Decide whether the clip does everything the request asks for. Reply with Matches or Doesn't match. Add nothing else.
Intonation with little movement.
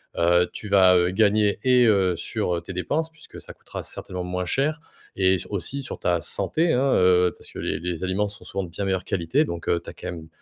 Doesn't match